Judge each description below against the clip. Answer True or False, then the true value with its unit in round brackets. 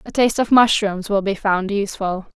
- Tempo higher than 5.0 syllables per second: True (5.5 syllables/s)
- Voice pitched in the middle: False (205 Hz)